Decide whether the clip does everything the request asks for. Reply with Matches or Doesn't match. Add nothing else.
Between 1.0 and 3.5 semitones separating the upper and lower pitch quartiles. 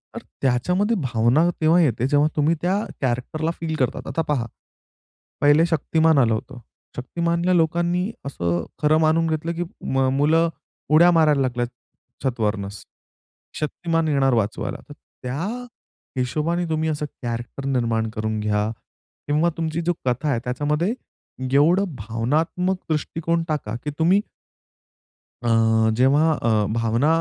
Doesn't match